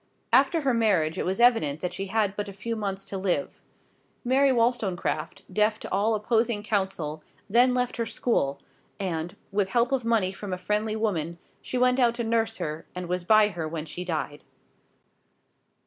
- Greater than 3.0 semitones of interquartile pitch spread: Yes, average, 4.4 semitones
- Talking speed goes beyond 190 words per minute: No, average, 180 wpm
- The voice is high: Yes, high, 210 Hz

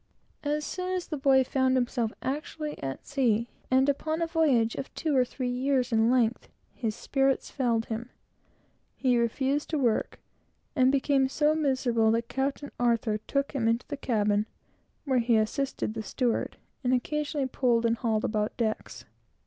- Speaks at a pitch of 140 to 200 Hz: No, very high, 255 Hz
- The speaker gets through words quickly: No, average, 165 wpm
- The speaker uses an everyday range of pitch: Yes, average, 3.3 semitones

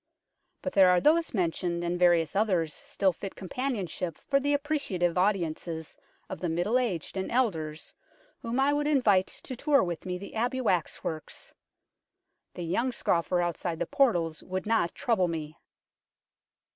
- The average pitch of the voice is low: No, medium, 185 Hz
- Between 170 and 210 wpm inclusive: No, average, 155 wpm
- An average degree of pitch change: No, wide, 6.4 semitones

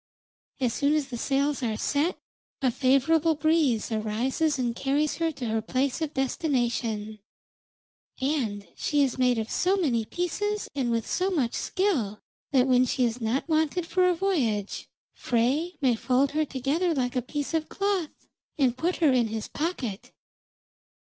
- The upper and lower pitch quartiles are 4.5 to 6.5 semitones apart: Yes, average, 4.9 semitones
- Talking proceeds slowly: No, average, 165 wpm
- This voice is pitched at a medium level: No, very high, 270 Hz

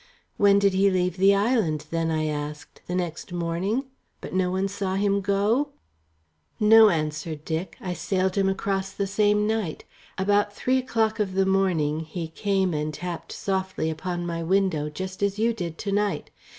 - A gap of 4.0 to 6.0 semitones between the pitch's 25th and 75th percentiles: No, average, 3.3 semitones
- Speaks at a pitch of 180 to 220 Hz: Yes, high, 190 Hz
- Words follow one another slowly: No, average, 175 wpm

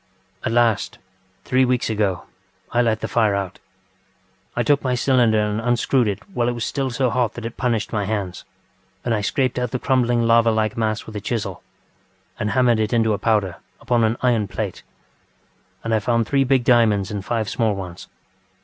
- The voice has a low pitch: Yes, low, 115 Hz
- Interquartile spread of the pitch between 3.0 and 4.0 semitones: No, narrow, 2.4 semitones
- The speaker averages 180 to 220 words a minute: Yes, average, 195 wpm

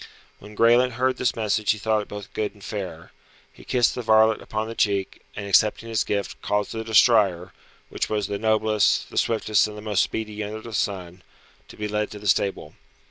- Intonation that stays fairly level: Yes, narrow, 1.5 semitones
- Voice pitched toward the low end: Yes, low, 105 Hz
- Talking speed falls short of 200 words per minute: No, fast, 205 wpm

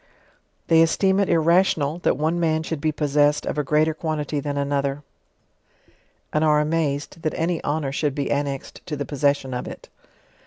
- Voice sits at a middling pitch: Yes, medium, 150 Hz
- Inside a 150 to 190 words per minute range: Yes, average, 180 wpm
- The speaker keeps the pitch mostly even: Yes, narrow, 2.1 semitones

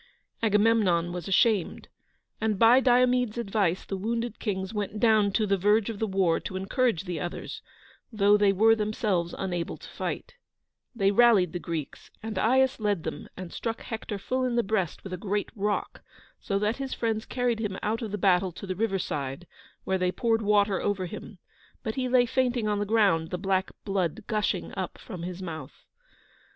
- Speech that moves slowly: No, average, 190 wpm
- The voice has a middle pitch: No, high, 205 Hz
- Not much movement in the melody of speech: No, average, 3.2 semitones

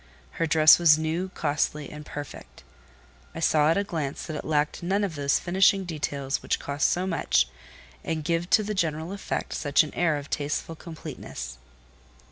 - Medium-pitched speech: Yes, medium, 155 Hz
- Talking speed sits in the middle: Yes, average, 175 wpm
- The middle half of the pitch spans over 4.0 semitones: No, average, 2.8 semitones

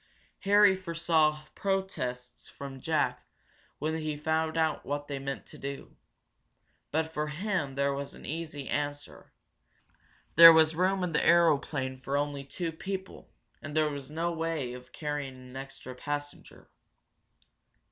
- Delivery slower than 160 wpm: Yes, average, 140 wpm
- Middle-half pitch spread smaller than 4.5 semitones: Yes, average, 2.9 semitones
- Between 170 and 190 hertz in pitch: No, medium, 150 Hz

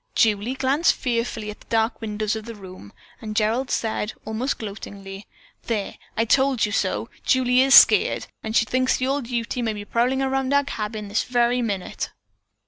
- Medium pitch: No, high, 230 Hz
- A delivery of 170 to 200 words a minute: Yes, average, 175 wpm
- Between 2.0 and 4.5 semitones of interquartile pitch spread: Yes, average, 3.3 semitones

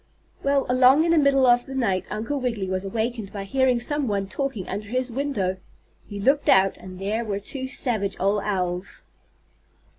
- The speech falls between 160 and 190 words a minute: Yes, average, 180 wpm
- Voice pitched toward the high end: Yes, high, 225 Hz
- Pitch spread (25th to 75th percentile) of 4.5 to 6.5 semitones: Yes, average, 5.2 semitones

